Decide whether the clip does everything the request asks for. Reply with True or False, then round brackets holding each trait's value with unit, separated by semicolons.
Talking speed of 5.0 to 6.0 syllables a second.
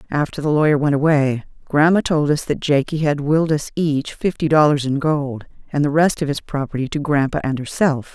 True (5.4 syllables/s)